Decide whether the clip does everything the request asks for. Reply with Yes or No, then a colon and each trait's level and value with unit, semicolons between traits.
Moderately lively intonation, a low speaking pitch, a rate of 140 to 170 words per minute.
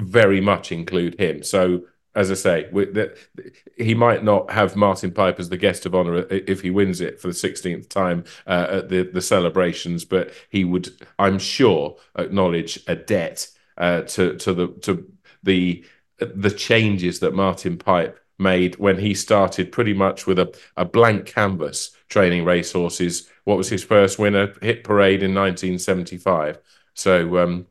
No: narrow, 1.9 semitones; very low, 95 Hz; average, 165 wpm